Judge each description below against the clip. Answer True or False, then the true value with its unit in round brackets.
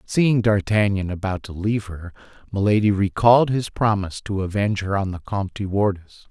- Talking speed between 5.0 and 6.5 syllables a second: True (5.8 syllables/s)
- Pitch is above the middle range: False (100 Hz)